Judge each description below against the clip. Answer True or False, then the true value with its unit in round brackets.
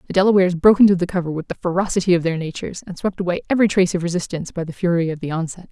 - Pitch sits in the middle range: True (180 Hz)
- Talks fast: True (265 wpm)